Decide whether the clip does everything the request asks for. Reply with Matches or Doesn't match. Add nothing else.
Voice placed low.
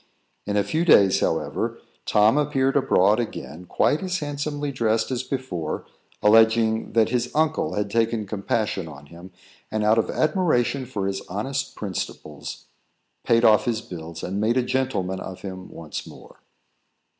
Matches